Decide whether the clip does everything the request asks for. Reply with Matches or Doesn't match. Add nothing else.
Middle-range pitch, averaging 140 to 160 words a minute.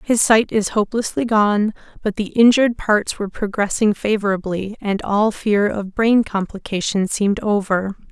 Doesn't match